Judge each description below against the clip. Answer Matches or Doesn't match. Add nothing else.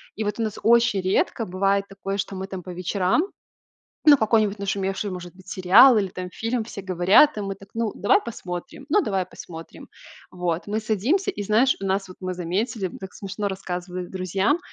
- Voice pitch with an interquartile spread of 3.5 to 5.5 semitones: Doesn't match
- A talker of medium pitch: Doesn't match